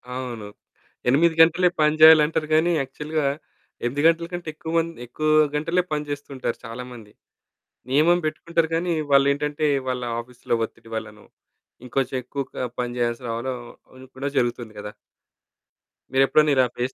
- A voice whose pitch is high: No, medium, 140 Hz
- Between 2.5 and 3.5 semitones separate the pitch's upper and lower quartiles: No, average, 4.2 semitones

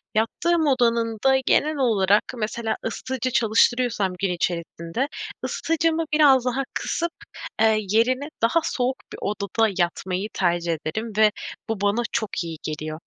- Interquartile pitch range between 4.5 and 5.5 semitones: Yes, average, 5.0 semitones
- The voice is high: Yes, high, 225 Hz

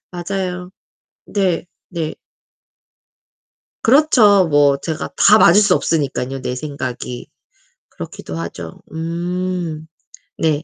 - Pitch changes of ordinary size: Yes, average, 4.4 semitones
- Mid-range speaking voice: Yes, medium, 165 Hz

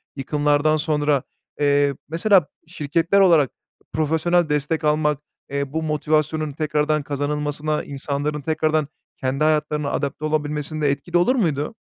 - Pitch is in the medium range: Yes, medium, 150 Hz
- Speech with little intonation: Yes, narrow, 1.4 semitones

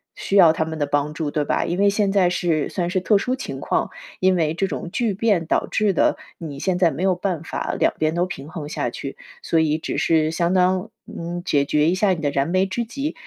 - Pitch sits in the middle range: Yes, medium, 175 Hz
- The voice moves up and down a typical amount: Yes, average, 3.5 semitones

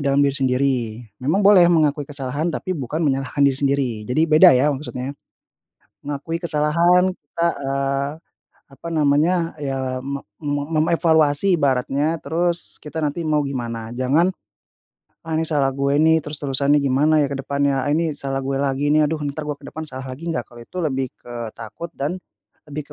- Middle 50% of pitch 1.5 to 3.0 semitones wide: Yes, average, 2.7 semitones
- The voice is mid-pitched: Yes, medium, 145 Hz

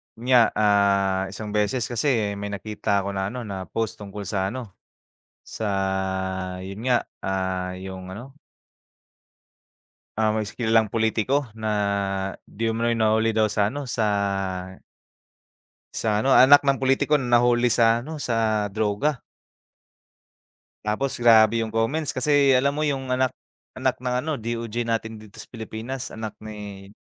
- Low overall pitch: Yes, low, 110 Hz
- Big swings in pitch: No, average, 3.4 semitones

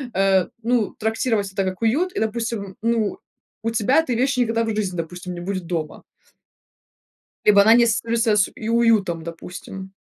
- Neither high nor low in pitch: No, high, 215 Hz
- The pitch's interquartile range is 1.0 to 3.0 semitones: No, average, 3.4 semitones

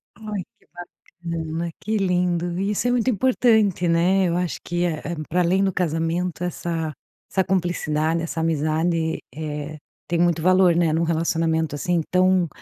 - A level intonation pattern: Yes, narrow, 2.2 semitones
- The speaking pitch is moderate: Yes, medium, 170 Hz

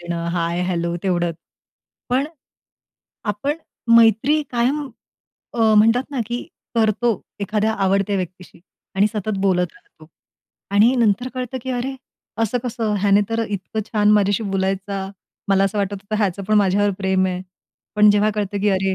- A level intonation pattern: No, average, 3.0 semitones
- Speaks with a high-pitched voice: Yes, high, 205 Hz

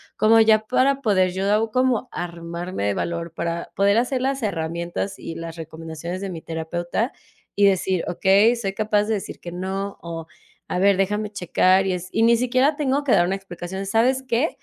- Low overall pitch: No, high, 195 Hz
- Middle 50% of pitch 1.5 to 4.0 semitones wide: No, average, 4.5 semitones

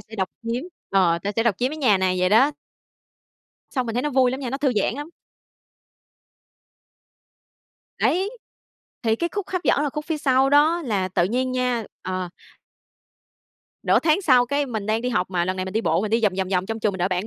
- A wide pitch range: Yes, wide, 6.1 semitones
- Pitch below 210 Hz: No, high, 230 Hz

